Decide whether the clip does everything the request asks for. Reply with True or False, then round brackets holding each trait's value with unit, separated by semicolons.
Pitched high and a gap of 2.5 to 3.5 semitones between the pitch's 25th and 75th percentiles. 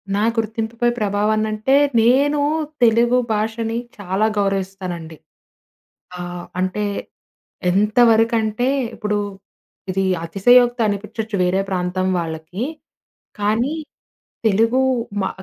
True (210 Hz; 3.2 semitones)